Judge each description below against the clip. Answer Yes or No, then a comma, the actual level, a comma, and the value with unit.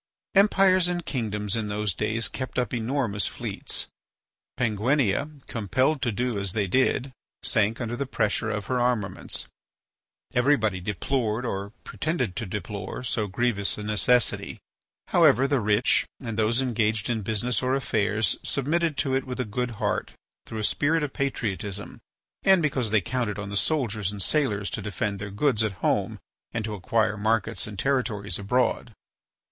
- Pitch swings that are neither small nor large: Yes, average, 3.8 semitones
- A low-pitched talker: Yes, low, 115 Hz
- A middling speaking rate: Yes, average, 160 wpm